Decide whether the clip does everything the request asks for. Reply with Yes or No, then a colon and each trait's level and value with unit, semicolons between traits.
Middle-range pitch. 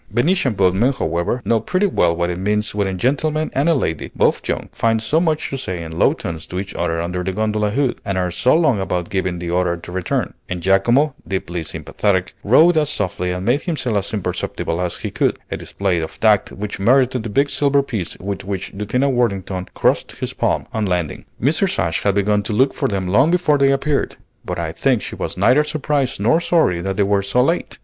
No: low, 105 Hz